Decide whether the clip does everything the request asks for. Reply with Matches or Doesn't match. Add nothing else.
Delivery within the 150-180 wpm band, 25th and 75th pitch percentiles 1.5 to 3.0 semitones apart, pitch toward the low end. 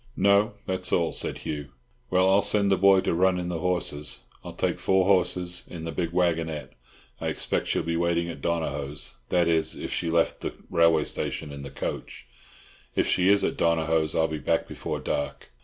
Doesn't match